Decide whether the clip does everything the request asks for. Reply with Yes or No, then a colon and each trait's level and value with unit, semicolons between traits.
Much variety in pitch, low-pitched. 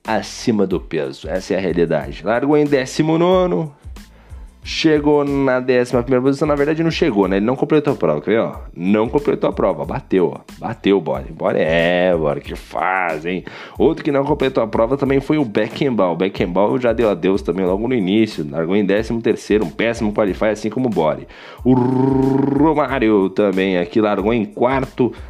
Yes: wide, 6.2 semitones; low, 125 Hz